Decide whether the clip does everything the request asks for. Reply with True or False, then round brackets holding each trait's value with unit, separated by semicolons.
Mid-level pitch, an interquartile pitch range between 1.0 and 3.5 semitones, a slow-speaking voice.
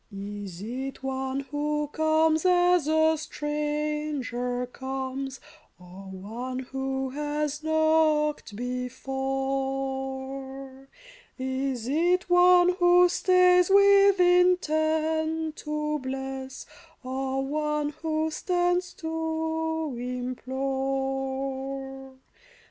False (275 Hz; 3.1 semitones; 80 wpm)